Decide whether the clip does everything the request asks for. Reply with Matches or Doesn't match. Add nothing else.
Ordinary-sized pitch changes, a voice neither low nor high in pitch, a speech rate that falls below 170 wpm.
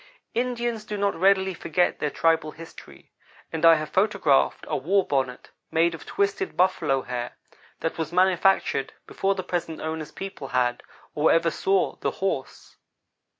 Matches